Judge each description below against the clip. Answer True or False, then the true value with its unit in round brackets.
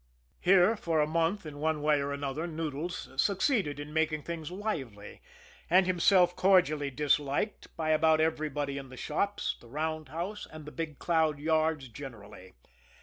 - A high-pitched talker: False (155 Hz)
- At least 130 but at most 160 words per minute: True (150 wpm)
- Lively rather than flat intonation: False (3.0 semitones)